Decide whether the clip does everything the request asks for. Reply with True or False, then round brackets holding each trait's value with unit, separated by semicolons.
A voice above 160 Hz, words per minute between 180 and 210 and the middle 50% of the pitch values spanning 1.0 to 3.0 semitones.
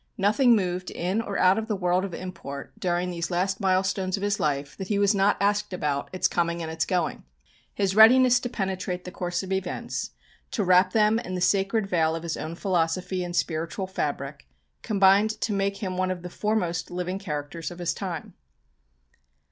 True (185 Hz; 195 wpm; 2.4 semitones)